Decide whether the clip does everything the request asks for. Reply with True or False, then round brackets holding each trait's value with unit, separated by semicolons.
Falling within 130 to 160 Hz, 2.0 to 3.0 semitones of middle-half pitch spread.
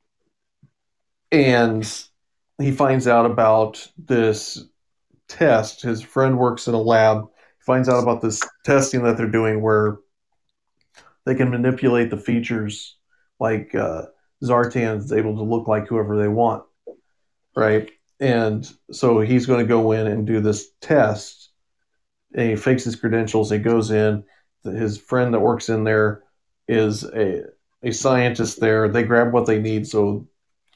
False (115 Hz; 2.4 semitones)